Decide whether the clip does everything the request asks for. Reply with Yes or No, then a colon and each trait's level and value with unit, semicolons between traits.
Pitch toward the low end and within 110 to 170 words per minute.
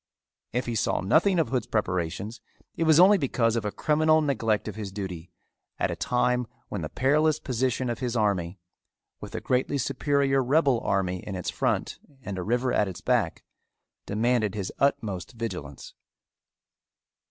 Yes: low, 120 Hz; average, 165 wpm